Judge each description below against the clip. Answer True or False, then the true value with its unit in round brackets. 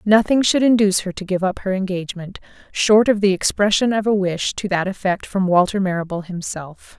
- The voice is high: True (195 Hz)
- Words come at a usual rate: True (190 wpm)